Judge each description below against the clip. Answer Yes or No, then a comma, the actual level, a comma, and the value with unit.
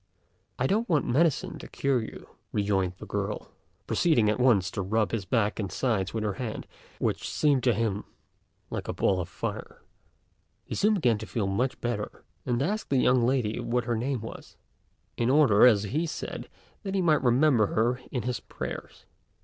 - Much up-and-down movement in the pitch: No, average, 4.3 semitones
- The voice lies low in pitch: Yes, low, 120 Hz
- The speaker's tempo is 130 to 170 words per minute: No, average, 190 wpm